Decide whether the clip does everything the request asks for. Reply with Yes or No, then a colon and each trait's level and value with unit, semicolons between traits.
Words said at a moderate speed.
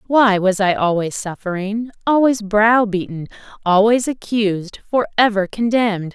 No: slow, 115 wpm